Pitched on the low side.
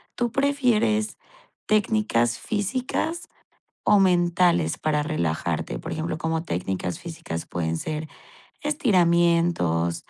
No: medium, 170 Hz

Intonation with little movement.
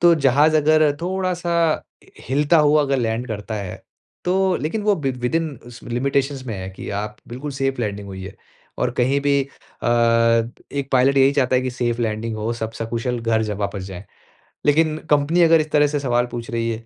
No: average, 4.7 semitones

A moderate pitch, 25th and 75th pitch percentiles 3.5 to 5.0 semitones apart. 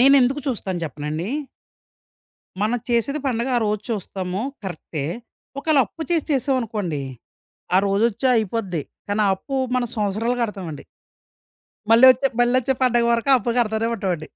No: high, 225 Hz; average, 4.7 semitones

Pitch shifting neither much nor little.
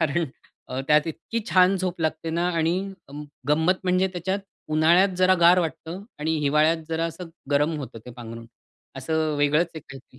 Yes: average, 3.1 semitones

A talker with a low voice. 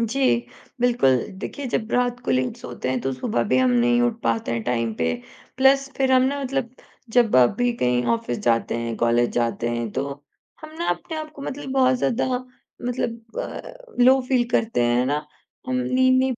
No: high, 240 Hz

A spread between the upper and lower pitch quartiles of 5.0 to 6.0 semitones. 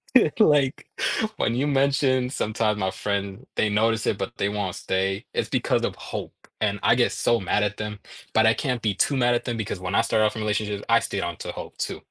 No: average, 3.1 semitones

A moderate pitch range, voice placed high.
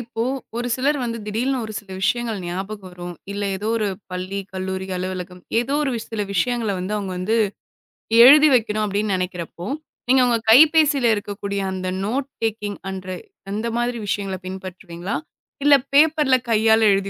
Yes: average, 4.3 semitones; high, 210 Hz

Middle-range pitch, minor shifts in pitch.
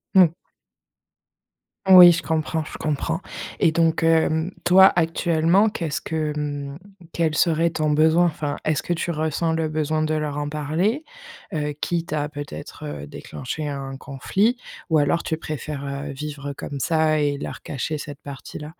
Yes: medium, 155 Hz; narrow, 2.2 semitones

